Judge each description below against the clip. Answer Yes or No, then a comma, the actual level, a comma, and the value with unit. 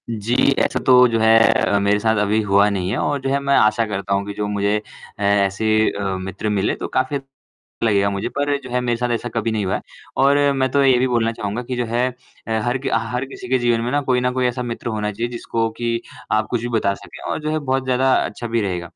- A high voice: No, low, 115 Hz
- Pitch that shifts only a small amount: No, average, 3.4 semitones